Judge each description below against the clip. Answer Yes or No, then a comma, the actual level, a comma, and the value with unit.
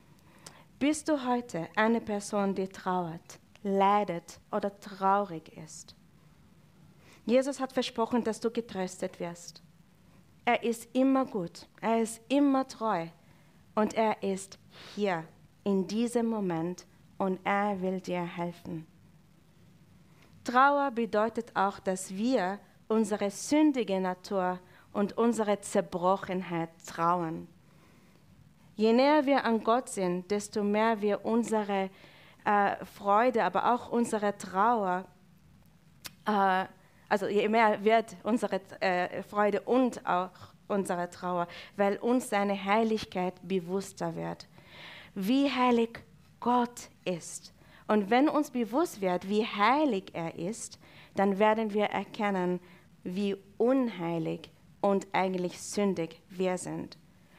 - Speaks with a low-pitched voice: No, high, 200 Hz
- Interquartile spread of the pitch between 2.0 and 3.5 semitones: No, average, 3.9 semitones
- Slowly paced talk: Yes, slow, 115 wpm